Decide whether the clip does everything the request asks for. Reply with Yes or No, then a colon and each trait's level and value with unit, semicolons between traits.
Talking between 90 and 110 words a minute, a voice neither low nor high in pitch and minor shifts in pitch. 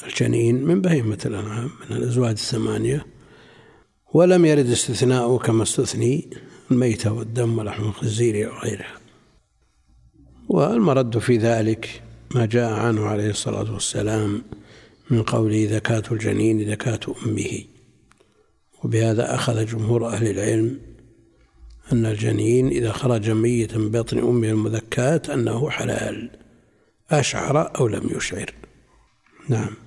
No: average, 105 wpm; low, 115 Hz; narrow, 1.9 semitones